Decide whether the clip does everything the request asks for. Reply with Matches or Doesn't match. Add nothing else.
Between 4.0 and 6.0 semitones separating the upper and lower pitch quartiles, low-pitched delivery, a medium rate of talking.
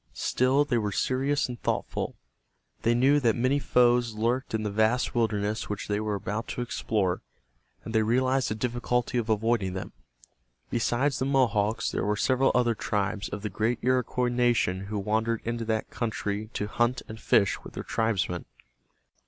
Doesn't match